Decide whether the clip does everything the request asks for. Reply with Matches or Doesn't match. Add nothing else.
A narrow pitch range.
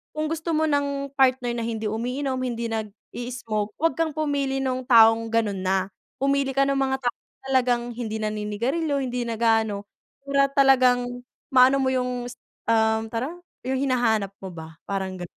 Doesn't match